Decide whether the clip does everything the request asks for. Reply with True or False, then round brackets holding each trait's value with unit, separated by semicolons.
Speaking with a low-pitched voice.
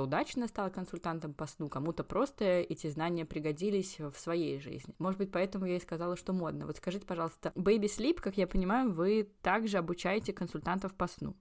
False (180 Hz)